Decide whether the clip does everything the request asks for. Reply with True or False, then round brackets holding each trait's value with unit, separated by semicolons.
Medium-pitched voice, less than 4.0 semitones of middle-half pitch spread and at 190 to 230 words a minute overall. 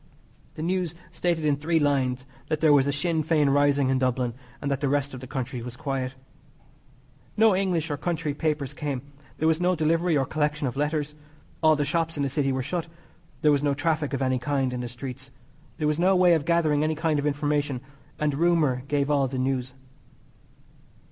True (145 Hz; 2.8 semitones; 205 wpm)